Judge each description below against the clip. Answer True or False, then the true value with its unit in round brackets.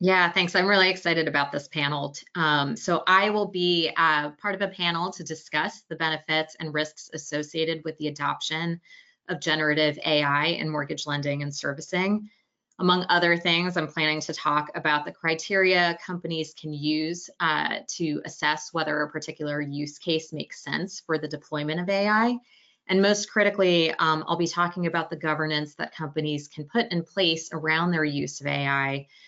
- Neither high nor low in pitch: True (160 Hz)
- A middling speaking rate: True (175 wpm)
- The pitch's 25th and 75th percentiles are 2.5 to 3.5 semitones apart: True (2.9 semitones)